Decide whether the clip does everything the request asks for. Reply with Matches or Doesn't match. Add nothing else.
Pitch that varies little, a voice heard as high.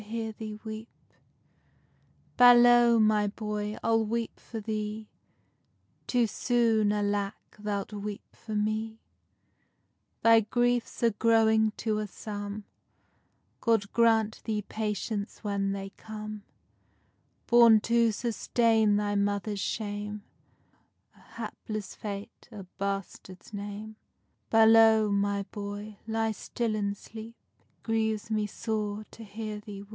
Matches